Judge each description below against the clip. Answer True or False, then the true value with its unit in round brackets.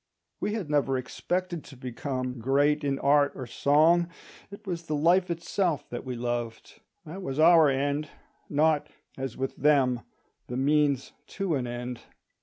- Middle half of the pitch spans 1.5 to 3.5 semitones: False (4.3 semitones)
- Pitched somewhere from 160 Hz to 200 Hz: False (145 Hz)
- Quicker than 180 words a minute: False (150 wpm)